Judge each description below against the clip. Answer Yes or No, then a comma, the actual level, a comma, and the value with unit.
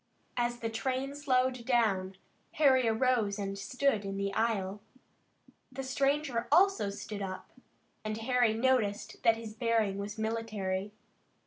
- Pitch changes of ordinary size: Yes, average, 4.0 semitones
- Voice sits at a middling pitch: No, high, 225 Hz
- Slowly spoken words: Yes, slow, 130 wpm